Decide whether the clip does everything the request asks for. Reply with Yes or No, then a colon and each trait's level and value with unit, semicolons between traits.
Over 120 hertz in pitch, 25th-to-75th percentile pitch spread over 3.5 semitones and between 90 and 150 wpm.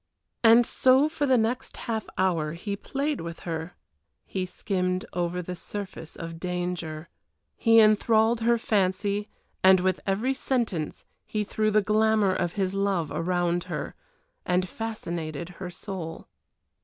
Yes: high, 190 Hz; average, 3.9 semitones; average, 140 wpm